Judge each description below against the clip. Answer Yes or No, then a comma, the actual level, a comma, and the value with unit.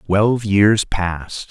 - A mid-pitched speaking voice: No, low, 100 Hz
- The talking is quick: No, slow, 120 wpm